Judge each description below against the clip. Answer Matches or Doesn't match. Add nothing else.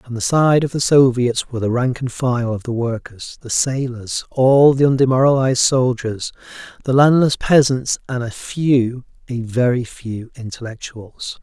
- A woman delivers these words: Doesn't match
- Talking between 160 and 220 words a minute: Doesn't match